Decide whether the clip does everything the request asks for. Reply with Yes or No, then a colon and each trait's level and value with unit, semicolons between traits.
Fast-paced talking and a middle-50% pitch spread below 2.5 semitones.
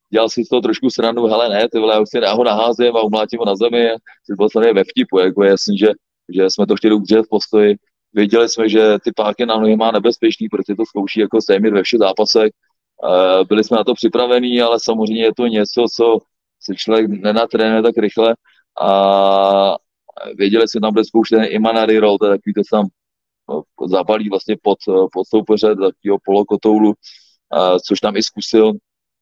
Yes: fast, 180 wpm; narrow, 1.8 semitones